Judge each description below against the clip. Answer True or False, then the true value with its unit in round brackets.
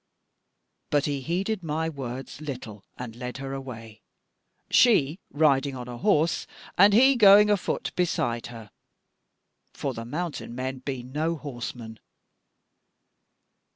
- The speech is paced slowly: True (120 wpm)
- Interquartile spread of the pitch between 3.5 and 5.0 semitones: False (5.4 semitones)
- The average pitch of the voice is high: False (135 Hz)